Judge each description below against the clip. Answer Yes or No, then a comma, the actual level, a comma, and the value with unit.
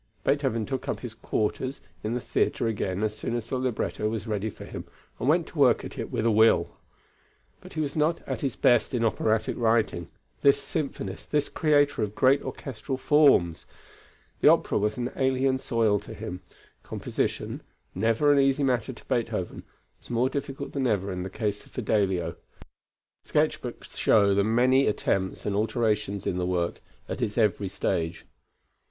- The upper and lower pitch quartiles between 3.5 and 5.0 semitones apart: Yes, average, 4.4 semitones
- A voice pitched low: Yes, low, 115 Hz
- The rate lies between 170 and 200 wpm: Yes, average, 180 wpm